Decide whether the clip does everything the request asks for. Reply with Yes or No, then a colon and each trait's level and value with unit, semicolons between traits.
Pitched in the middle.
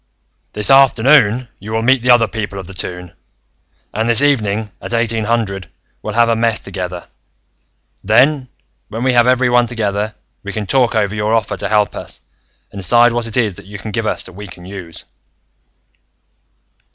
No: low, 110 Hz